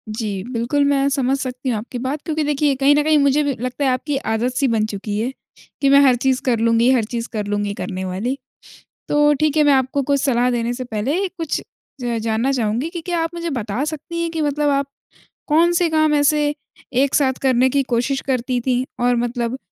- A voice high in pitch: Yes, very high, 265 Hz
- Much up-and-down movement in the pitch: No, average, 3.8 semitones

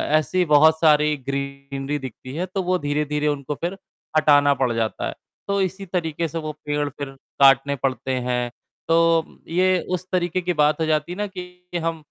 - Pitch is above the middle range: No, medium, 150 Hz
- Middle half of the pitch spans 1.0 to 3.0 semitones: No, average, 4.1 semitones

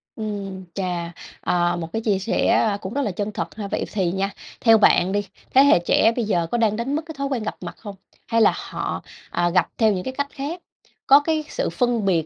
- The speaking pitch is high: Yes, high, 210 Hz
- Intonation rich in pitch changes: No, average, 4.6 semitones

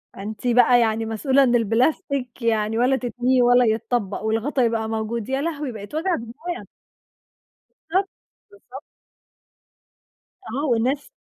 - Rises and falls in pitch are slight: No, average, 3.3 semitones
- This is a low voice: No, high, 245 Hz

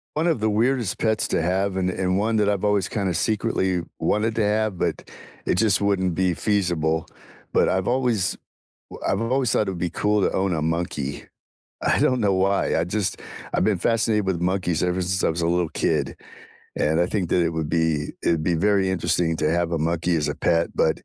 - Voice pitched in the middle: No, very low, 95 Hz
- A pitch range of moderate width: Yes, average, 3.5 semitones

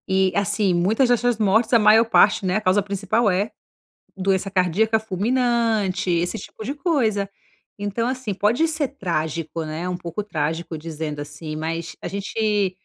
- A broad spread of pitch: No, average, 4.0 semitones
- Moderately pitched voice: No, high, 200 Hz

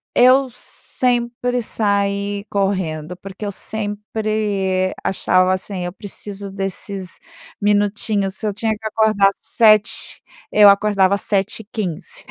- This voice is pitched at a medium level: No, high, 205 Hz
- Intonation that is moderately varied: No, narrow, 2.0 semitones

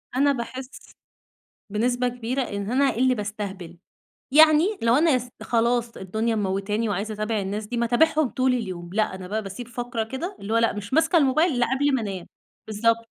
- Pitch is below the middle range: No, high, 230 Hz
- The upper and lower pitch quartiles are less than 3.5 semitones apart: No, average, 3.9 semitones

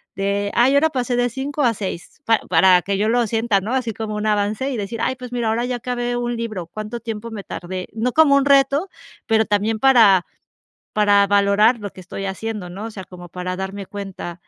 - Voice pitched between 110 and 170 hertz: No, high, 220 Hz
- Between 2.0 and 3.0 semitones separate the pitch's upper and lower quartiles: No, average, 3.5 semitones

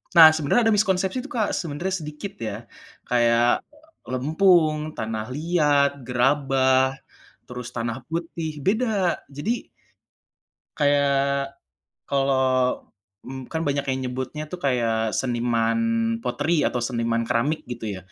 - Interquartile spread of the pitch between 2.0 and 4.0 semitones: No, average, 4.6 semitones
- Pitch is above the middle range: No, medium, 140 Hz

